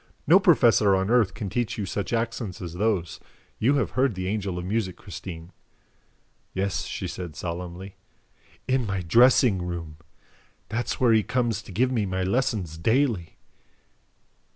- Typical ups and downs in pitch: Yes, average, 4.7 semitones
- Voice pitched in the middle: No, low, 100 Hz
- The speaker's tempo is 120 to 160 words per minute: Yes, average, 155 wpm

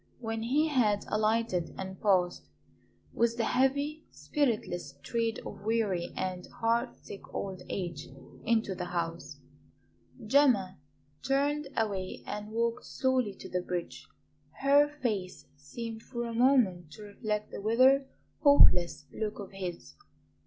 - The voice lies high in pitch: Yes, high, 220 Hz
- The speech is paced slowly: Yes, slow, 130 wpm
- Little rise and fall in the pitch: No, average, 5.1 semitones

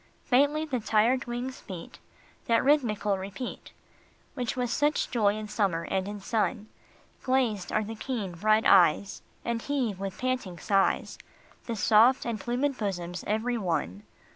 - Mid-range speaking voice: No, high, 220 Hz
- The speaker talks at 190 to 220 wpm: No, average, 145 wpm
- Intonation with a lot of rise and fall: No, average, 4.1 semitones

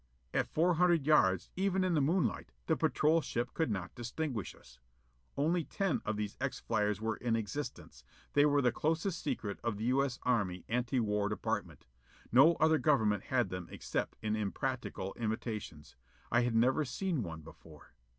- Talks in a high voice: No, low, 120 Hz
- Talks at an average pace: Yes, average, 170 wpm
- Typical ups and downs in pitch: No, wide, 6.7 semitones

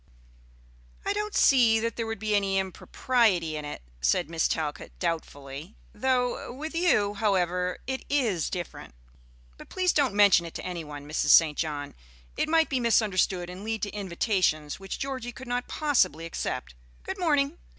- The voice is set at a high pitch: Yes, high, 205 Hz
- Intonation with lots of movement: Yes, wide, 7.1 semitones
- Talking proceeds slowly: No, average, 165 wpm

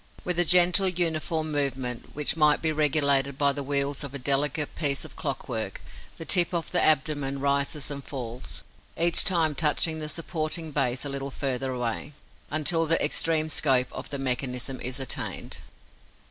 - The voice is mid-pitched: Yes, medium, 145 Hz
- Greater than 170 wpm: No, average, 165 wpm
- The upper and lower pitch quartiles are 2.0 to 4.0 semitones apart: Yes, average, 2.7 semitones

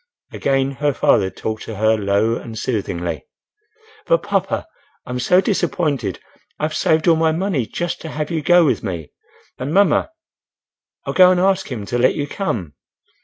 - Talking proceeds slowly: No, average, 155 wpm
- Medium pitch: Yes, medium, 145 Hz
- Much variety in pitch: Yes, wide, 8.0 semitones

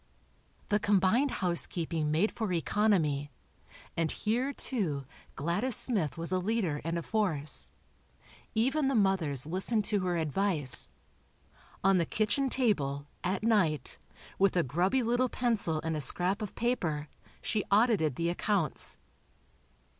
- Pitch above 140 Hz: Yes, medium, 185 Hz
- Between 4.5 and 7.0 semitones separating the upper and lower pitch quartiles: Yes, wide, 5.4 semitones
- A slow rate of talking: Yes, slow, 130 wpm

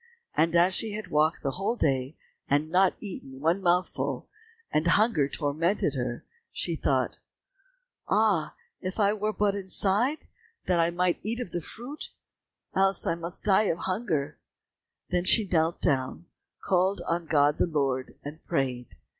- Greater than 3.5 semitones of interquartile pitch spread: Yes, average, 4.7 semitones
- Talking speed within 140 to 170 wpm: Yes, average, 155 wpm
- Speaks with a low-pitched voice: No, medium, 175 Hz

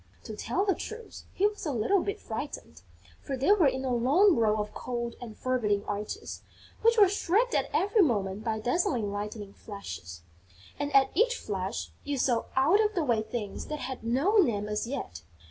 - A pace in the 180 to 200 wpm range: Yes, average, 190 wpm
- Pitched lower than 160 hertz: No, very high, 250 Hz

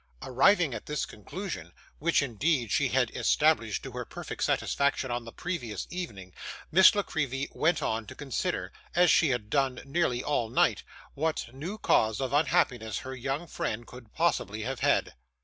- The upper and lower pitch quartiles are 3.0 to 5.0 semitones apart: No, wide, 5.4 semitones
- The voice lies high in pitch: No, low, 135 Hz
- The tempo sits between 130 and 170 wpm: Yes, average, 165 wpm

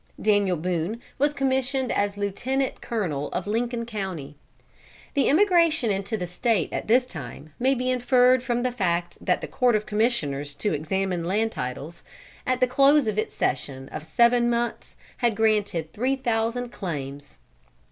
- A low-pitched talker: No, high, 220 Hz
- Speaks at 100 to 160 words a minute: Yes, average, 155 wpm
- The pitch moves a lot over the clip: Yes, wide, 6.2 semitones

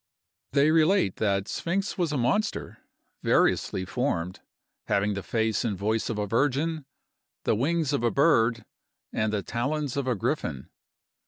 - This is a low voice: Yes, low, 120 Hz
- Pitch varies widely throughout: Yes, wide, 6.3 semitones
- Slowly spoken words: No, average, 150 wpm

